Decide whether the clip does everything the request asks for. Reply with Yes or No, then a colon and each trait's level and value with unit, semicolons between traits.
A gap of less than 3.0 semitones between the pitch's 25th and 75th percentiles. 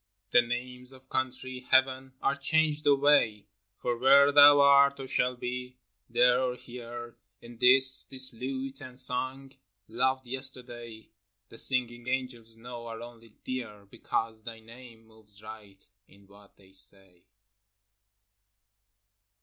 Yes: narrow, 2.5 semitones